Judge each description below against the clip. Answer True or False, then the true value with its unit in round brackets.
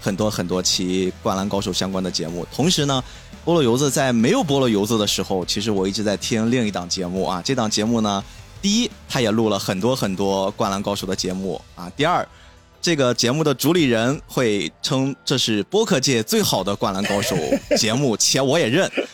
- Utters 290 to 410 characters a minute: True (305 characters per minute)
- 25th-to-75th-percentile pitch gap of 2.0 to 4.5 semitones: False (5.3 semitones)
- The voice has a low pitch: True (105 Hz)